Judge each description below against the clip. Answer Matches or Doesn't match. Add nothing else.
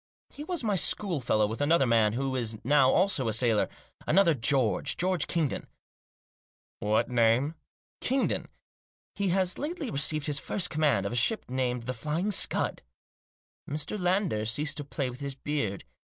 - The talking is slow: Doesn't match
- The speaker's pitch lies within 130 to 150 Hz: Matches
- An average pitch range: Doesn't match